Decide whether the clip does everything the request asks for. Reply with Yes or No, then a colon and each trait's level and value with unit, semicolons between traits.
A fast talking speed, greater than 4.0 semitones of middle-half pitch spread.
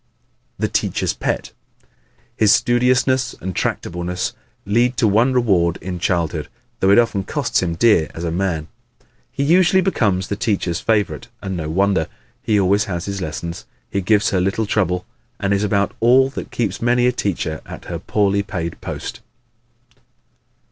No: average, 160 wpm; average, 4.6 semitones